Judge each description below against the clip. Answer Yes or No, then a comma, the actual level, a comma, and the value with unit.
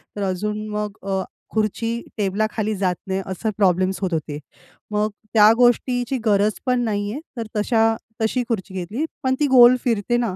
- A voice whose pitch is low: No, high, 210 Hz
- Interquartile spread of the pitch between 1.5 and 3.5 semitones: Yes, average, 3.2 semitones